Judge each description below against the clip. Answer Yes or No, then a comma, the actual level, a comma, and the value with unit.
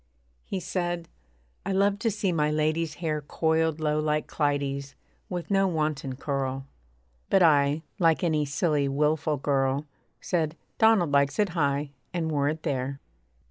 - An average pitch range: Yes, average, 3.2 semitones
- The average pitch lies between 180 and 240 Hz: No, medium, 155 Hz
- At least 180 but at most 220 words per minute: No, average, 145 wpm